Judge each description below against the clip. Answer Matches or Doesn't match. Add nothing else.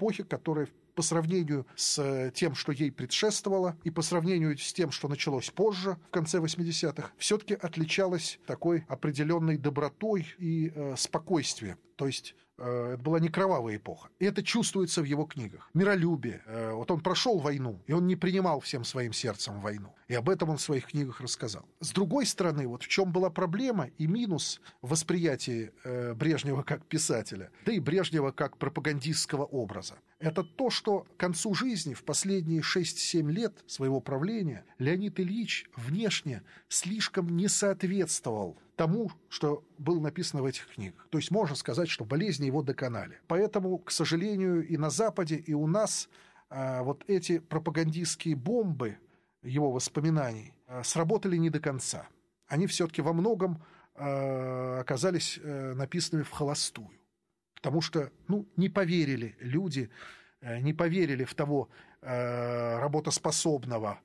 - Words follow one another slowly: Doesn't match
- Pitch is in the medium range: Matches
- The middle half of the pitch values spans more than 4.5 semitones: Matches